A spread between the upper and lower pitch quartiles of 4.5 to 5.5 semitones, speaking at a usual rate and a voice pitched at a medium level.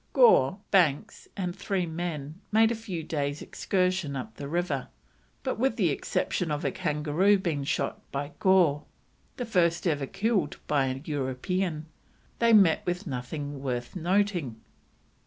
Yes: average, 5.1 semitones; average, 145 wpm; medium, 165 Hz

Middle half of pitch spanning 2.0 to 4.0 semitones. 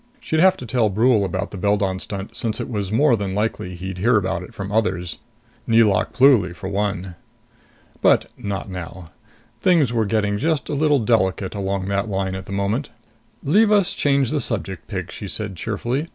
No: average, 4.5 semitones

